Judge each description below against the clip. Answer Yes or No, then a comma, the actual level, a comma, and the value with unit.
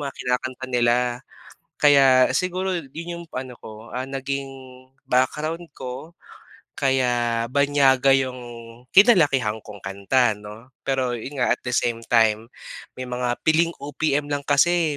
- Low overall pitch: Yes, low, 130 Hz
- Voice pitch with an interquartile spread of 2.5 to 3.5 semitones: Yes, average, 2.9 semitones